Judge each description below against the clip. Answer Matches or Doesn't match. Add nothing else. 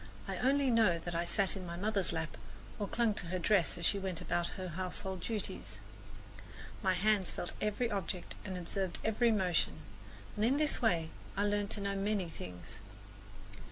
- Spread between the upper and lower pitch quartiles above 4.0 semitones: Doesn't match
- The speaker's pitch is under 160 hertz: Doesn't match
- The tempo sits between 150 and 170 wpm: Doesn't match